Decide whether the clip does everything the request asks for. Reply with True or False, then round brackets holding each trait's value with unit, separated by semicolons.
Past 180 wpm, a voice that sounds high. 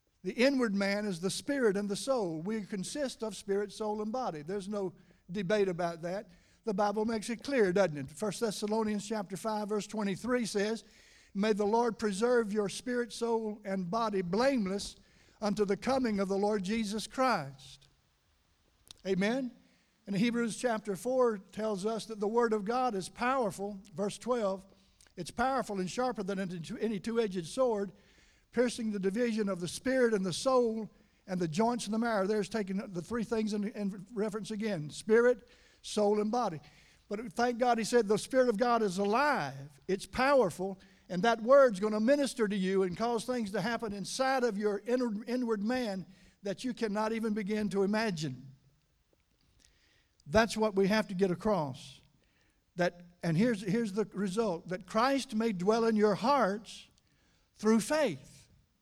False (165 wpm; 215 Hz)